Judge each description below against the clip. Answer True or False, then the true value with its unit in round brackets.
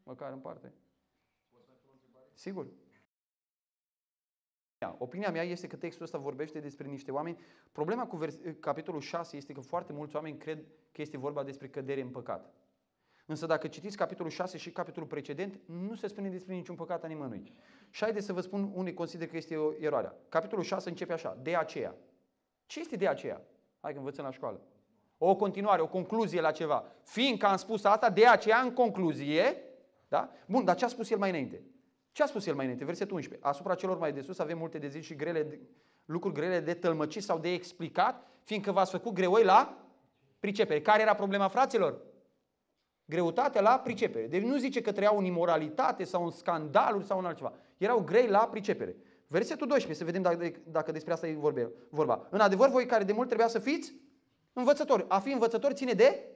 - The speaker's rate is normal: False (190 wpm)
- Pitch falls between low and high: True (180 Hz)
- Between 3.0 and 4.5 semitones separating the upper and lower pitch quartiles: False (5.3 semitones)